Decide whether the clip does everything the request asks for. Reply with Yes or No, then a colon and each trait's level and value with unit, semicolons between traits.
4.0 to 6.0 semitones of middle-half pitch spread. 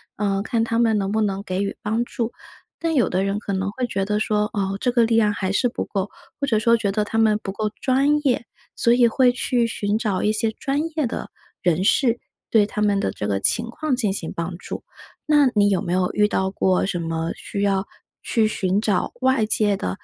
No: average, 3.2 semitones